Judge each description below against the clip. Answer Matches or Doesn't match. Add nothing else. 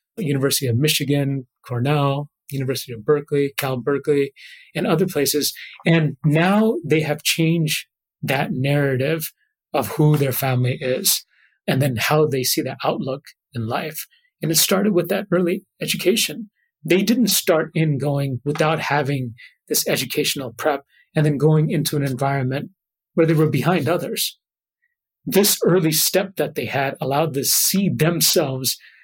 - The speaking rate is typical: Matches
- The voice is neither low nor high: Matches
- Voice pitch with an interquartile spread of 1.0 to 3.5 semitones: Doesn't match